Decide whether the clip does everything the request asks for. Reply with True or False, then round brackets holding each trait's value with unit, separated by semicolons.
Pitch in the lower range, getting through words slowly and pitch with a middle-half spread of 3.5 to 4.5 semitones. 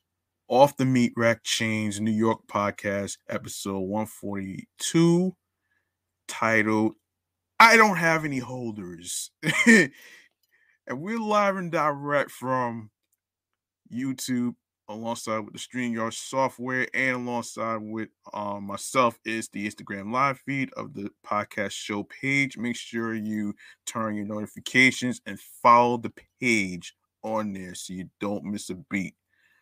True (110 Hz; 125 wpm; 4.2 semitones)